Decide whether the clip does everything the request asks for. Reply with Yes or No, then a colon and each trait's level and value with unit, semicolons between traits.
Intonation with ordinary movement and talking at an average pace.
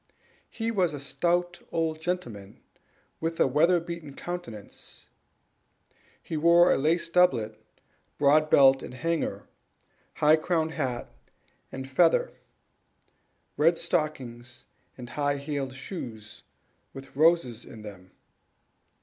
No: average, 4.7 semitones; slow, 110 wpm